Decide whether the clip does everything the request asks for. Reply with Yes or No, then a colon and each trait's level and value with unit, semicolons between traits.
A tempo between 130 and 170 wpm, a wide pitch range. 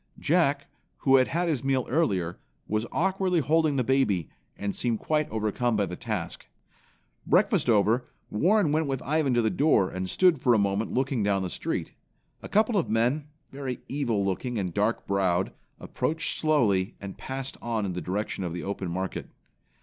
No: average, 180 wpm; wide, 6.7 semitones